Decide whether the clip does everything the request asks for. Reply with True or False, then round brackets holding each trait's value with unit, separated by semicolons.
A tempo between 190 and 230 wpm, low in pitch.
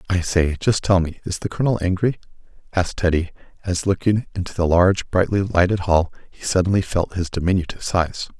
False (180 wpm; 90 Hz)